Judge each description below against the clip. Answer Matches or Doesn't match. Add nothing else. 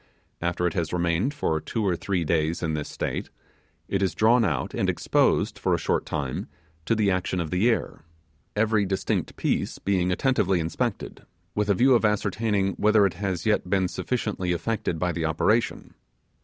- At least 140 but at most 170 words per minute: Doesn't match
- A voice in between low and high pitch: Doesn't match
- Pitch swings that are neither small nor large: Matches